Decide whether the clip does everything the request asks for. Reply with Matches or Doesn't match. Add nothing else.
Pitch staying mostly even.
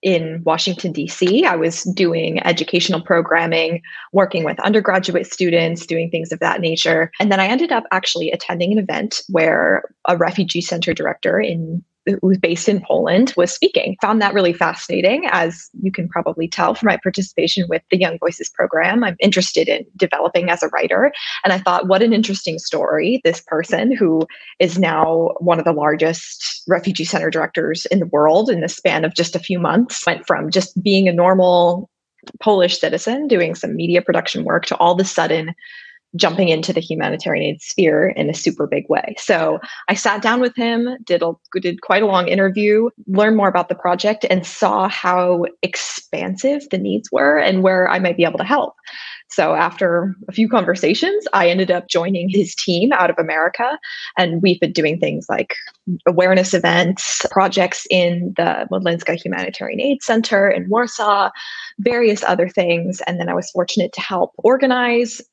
Doesn't match